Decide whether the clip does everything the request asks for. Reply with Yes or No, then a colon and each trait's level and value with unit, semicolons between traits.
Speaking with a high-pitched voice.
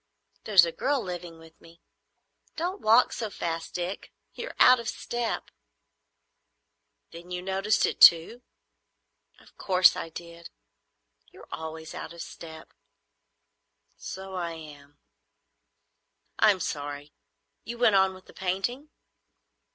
No: medium, 180 Hz